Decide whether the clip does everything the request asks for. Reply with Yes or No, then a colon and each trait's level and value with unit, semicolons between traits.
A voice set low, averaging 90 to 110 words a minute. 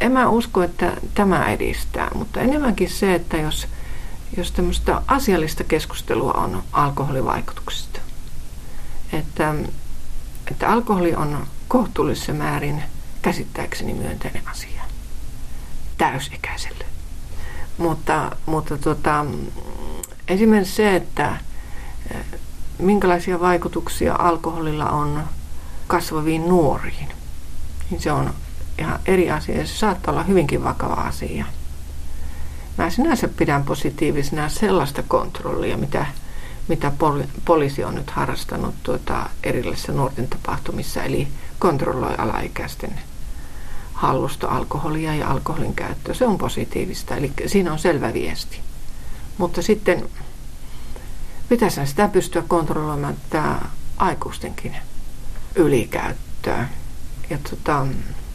No: medium, 150 Hz; average, 100 wpm